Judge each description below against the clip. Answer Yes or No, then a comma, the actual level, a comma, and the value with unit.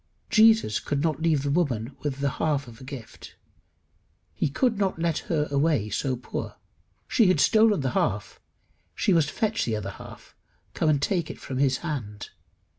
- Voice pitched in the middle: Yes, medium, 145 Hz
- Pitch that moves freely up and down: No, average, 4.8 semitones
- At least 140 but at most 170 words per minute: No, average, 180 wpm